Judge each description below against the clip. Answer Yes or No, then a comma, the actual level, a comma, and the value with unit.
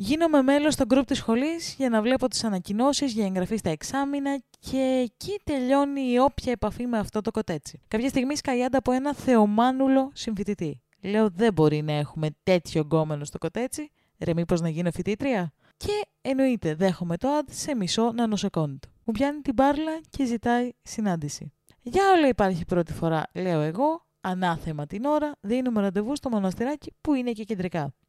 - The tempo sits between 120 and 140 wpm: No, fast, 170 wpm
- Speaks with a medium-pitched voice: No, high, 230 Hz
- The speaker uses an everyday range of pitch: No, wide, 7.3 semitones